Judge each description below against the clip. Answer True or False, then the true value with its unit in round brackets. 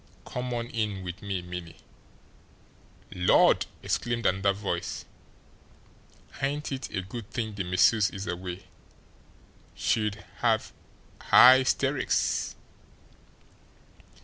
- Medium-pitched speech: False (100 Hz)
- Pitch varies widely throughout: False (4.3 semitones)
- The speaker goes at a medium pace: False (95 wpm)